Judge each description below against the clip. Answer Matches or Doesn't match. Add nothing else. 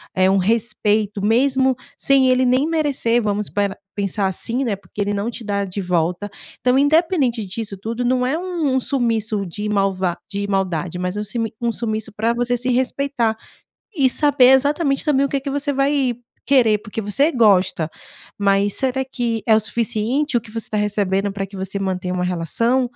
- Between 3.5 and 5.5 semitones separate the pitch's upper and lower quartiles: Matches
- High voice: Matches